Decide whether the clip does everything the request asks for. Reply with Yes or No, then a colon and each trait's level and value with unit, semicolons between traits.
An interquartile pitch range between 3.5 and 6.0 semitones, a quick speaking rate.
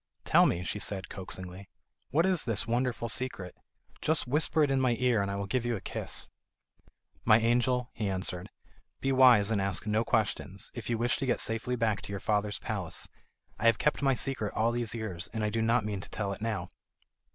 Yes: average, 3.8 semitones; fast, 210 wpm